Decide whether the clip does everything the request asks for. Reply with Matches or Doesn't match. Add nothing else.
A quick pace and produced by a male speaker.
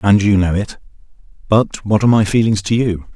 Matches